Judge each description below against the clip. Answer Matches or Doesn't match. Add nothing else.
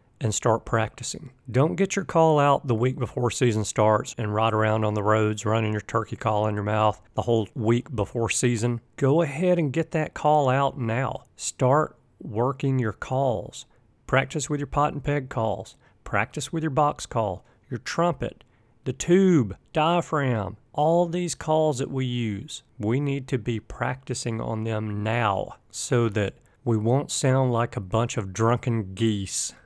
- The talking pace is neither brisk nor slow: Matches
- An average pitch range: Matches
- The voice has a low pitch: Matches